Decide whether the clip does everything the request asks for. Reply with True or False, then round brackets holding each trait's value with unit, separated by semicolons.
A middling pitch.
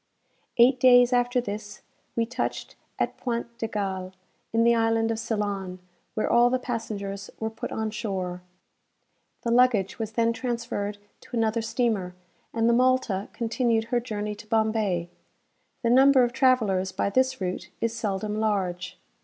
False (225 Hz)